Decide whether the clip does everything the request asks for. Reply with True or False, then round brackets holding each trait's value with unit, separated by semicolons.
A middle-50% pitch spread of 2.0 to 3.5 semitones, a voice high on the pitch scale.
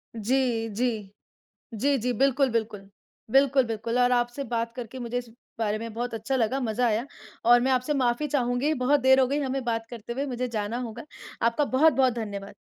True (2.6 semitones; 245 Hz)